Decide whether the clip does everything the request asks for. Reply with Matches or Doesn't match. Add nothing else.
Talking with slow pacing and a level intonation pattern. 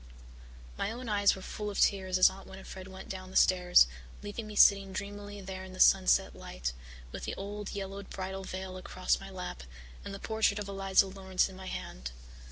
Doesn't match